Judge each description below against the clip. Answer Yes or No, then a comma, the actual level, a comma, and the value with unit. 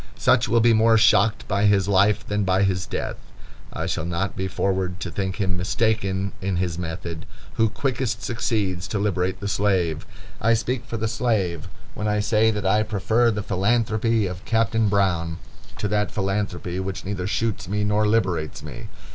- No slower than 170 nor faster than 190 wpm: Yes, average, 180 wpm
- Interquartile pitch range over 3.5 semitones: No, average, 3.0 semitones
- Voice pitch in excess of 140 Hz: No, low, 100 Hz